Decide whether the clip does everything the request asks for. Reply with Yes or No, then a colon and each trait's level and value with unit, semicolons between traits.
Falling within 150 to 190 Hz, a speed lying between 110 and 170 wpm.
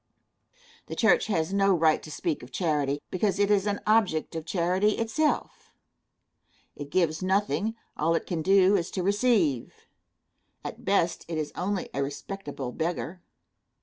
Yes: medium, 185 Hz; average, 150 wpm